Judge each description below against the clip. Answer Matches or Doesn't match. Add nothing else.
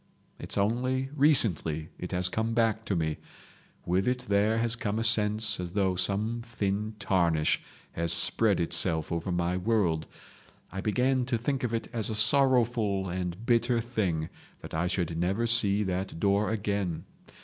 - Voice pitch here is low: Matches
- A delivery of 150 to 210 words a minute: Matches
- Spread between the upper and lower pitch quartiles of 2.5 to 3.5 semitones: Doesn't match